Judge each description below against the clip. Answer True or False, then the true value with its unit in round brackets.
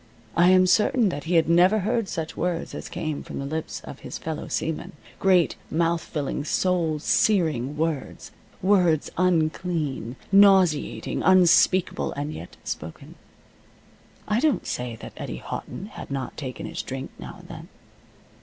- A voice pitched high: False (165 Hz)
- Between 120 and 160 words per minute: True (150 wpm)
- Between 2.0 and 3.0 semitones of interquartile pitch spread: False (3.7 semitones)